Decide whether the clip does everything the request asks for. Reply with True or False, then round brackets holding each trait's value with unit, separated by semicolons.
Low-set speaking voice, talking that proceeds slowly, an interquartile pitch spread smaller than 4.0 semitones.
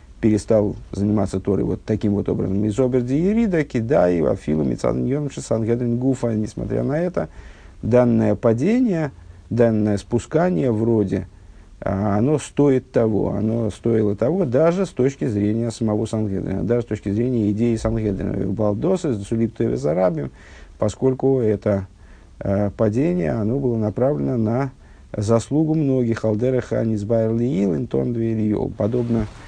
False (110 Hz; 120 wpm; 3.5 semitones)